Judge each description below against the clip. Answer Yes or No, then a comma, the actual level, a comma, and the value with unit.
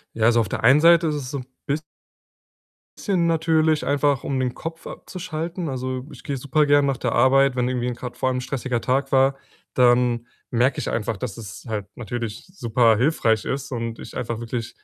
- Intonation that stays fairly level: No, average, 3.4 semitones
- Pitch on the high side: No, low, 130 Hz